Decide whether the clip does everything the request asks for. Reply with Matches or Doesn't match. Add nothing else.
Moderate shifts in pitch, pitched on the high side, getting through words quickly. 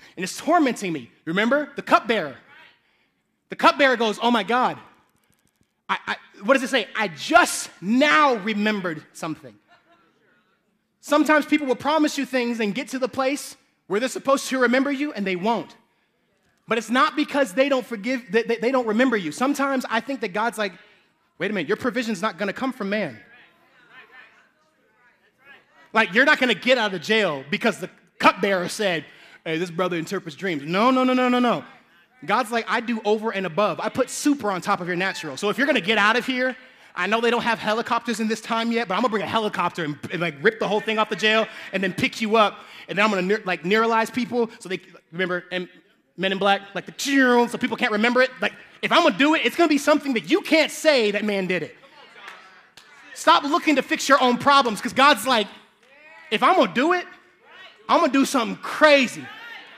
Matches